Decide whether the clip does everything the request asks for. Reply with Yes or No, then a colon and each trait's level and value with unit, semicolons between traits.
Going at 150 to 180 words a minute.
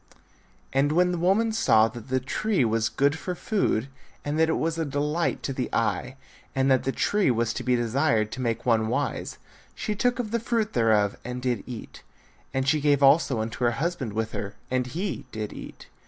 No: fast, 205 wpm